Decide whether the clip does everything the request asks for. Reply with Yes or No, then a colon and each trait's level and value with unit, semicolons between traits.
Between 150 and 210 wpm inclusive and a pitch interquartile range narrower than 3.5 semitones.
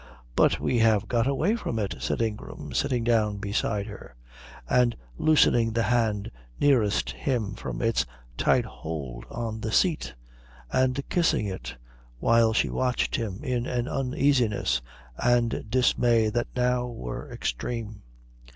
No: slow, 135 wpm; average, 2.9 semitones